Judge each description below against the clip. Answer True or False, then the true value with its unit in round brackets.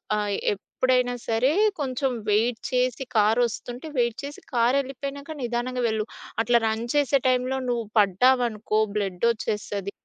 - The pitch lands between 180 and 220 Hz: False (240 Hz)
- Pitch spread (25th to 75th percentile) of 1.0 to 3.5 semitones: True (2.9 semitones)